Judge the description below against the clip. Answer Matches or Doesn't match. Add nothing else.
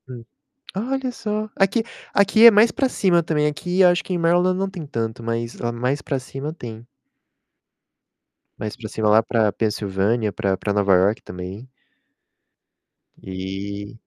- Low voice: Matches